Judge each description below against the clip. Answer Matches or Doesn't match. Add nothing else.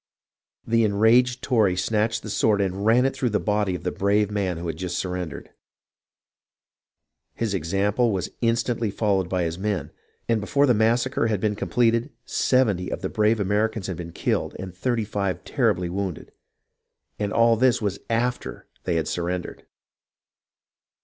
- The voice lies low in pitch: Matches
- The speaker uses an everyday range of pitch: Matches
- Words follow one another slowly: Doesn't match